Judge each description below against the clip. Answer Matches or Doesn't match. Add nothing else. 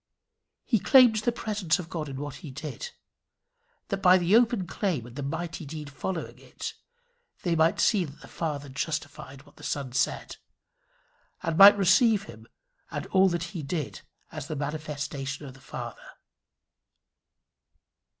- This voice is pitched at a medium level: Matches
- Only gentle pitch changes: Doesn't match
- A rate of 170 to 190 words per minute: Doesn't match